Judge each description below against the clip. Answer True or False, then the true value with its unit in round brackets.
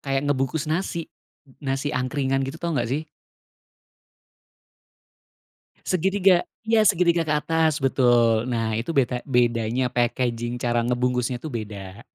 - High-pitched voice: False (130 Hz)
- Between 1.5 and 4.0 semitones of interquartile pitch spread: False (4.7 semitones)